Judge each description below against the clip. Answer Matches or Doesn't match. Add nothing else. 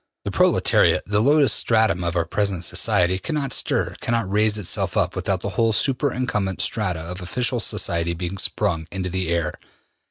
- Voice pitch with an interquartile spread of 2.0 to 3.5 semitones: Doesn't match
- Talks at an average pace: Matches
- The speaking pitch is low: Matches